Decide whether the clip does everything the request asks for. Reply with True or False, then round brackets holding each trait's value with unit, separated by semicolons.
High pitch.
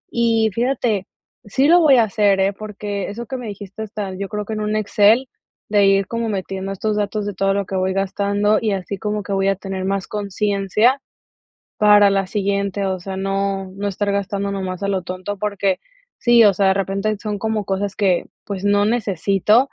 True (200 Hz)